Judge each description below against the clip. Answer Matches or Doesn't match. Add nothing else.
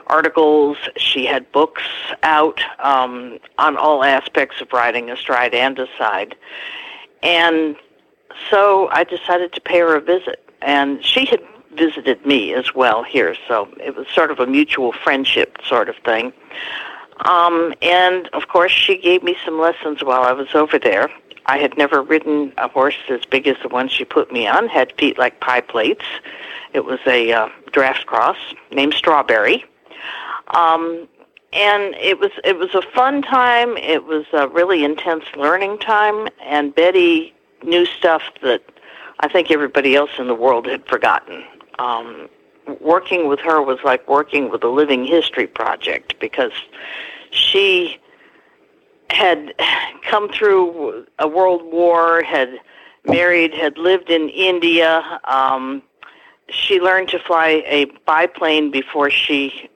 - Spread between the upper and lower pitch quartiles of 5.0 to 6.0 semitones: Matches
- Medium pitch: Matches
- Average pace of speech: Matches